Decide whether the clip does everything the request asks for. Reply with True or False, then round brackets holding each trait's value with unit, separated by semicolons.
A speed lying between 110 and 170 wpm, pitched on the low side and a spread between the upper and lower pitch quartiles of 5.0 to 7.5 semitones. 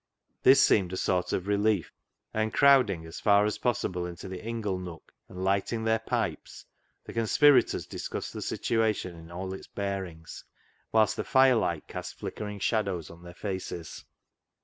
False (165 wpm; 100 Hz; 3.7 semitones)